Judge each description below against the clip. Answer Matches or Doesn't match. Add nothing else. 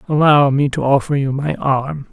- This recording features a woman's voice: Matches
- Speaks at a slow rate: Doesn't match